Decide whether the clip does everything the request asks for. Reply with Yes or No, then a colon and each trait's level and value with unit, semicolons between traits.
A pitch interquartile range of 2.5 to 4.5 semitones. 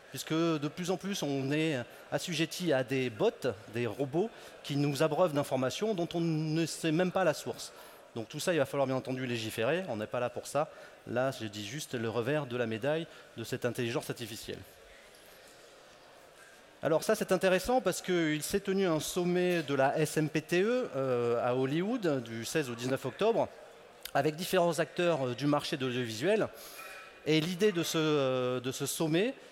No: average, 5.1 semitones